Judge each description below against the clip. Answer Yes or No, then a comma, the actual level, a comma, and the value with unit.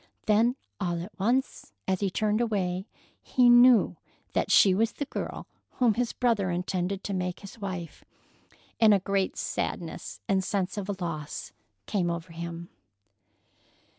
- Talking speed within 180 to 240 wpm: No, average, 150 wpm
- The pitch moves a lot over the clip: No, average, 3.4 semitones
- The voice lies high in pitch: Yes, high, 195 Hz